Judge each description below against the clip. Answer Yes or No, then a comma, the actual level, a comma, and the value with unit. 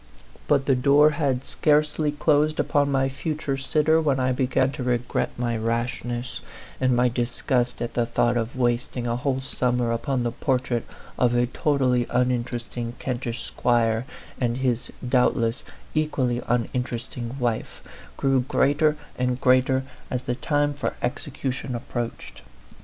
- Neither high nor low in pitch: No, low, 125 Hz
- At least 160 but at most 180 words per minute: No, average, 145 wpm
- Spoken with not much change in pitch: Yes, narrow, 2.2 semitones